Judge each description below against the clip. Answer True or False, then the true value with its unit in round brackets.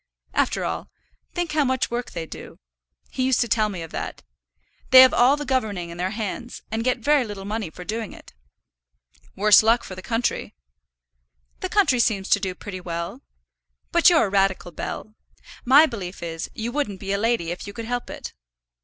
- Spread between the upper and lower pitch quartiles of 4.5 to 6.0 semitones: True (4.8 semitones)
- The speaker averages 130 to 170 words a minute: False (195 wpm)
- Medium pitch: False (220 Hz)